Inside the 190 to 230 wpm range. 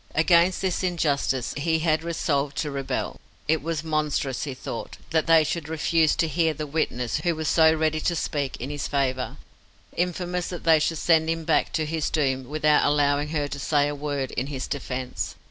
Yes: average, 195 wpm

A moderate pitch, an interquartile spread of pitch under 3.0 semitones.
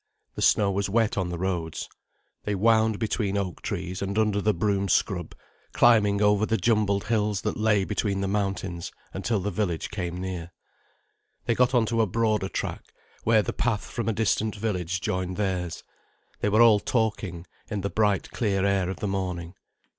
No: low, 100 Hz; narrow, 2.5 semitones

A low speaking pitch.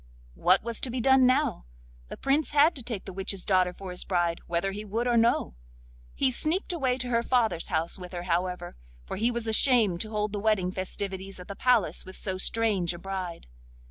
No: high, 205 Hz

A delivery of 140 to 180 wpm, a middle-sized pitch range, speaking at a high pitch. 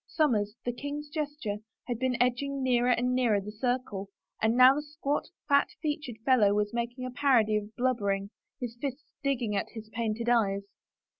Yes: average, 170 wpm; average, 4.2 semitones; high, 245 Hz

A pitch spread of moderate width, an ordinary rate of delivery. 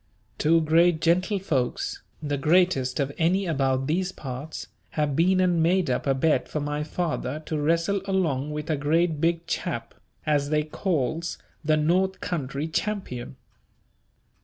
Yes: average, 3.2 semitones; average, 145 wpm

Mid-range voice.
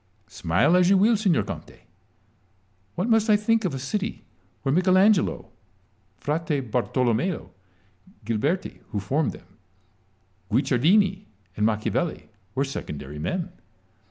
Yes: medium, 160 Hz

